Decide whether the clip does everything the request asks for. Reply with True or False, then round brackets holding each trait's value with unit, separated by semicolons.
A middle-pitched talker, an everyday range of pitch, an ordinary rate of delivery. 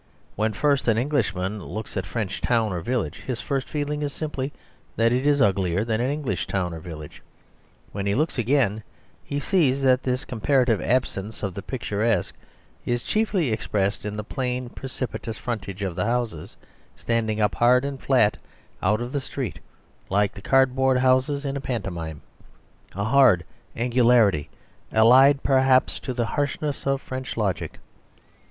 False (120 Hz; 4.5 semitones; 160 wpm)